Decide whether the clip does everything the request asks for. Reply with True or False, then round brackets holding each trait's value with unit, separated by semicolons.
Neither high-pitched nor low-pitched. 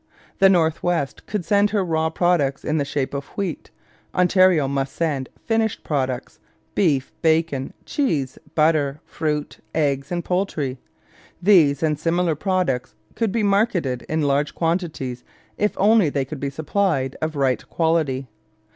True (160 Hz)